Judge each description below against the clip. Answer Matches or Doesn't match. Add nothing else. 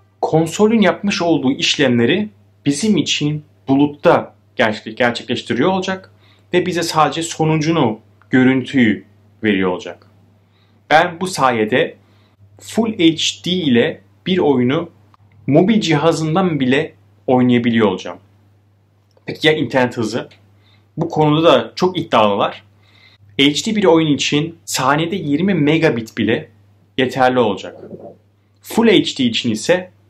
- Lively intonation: Matches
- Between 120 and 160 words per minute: Doesn't match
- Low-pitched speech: Matches